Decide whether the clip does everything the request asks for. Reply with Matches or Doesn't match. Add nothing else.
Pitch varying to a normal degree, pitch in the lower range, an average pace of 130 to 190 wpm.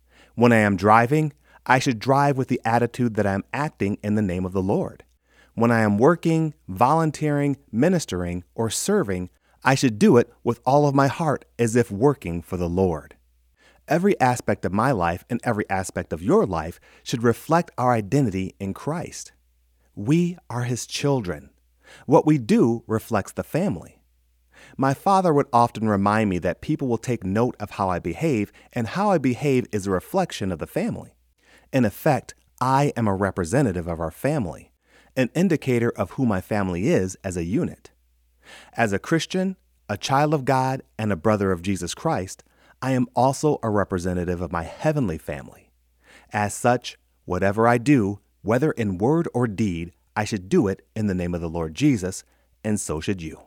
Doesn't match